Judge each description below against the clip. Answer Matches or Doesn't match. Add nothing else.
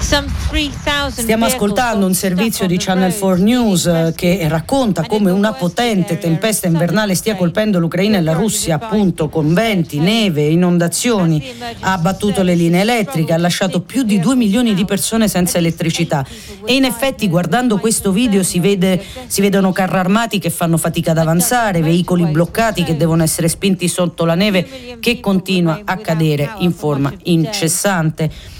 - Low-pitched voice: Doesn't match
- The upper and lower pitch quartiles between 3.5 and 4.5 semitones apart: Matches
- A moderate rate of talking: Matches